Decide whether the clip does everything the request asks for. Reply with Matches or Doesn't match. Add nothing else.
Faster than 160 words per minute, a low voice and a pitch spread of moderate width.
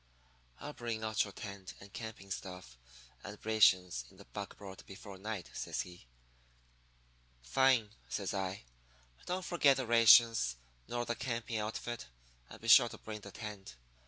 Doesn't match